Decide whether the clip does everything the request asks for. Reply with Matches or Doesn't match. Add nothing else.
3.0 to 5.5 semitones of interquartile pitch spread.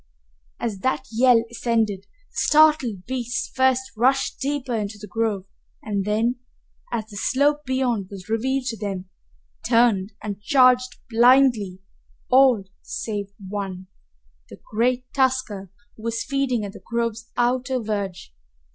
Matches